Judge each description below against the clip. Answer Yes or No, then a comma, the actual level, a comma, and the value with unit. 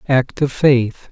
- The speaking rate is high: No, average, 160 wpm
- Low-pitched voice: Yes, low, 130 Hz